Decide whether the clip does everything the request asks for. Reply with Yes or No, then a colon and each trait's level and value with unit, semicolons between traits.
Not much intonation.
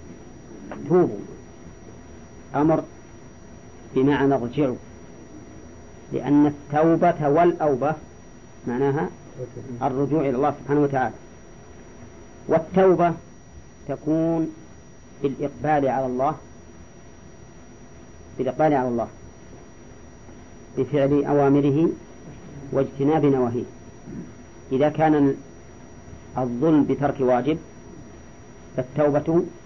No: average, 3.1 semitones